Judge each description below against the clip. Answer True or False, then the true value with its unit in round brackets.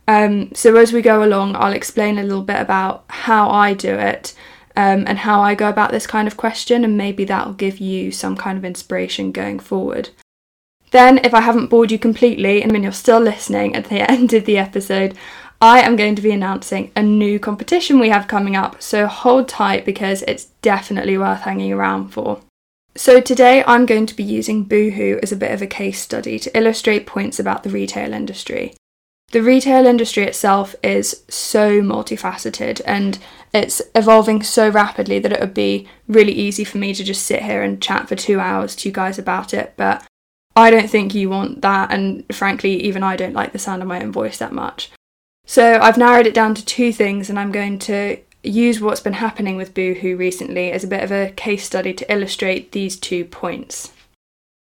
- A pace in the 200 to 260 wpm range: True (205 wpm)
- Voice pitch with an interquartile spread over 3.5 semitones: False (2.8 semitones)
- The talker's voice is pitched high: True (205 Hz)